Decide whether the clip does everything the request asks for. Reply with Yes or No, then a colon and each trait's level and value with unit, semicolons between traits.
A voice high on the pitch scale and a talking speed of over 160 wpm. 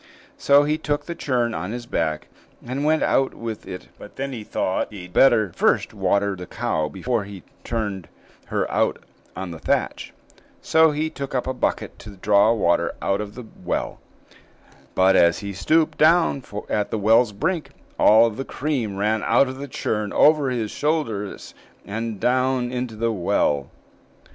No: low, 115 Hz; average, 175 wpm